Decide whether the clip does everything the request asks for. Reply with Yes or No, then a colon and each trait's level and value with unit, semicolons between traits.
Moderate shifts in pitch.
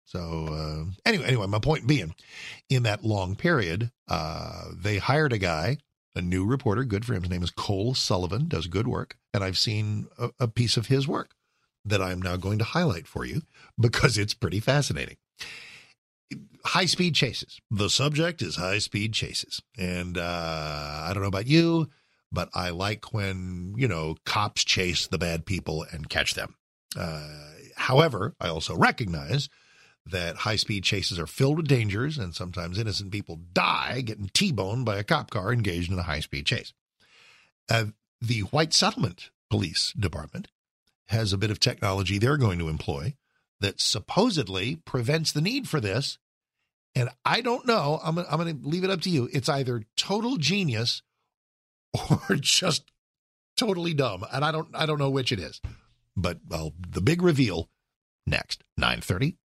No: wide, 7.1 semitones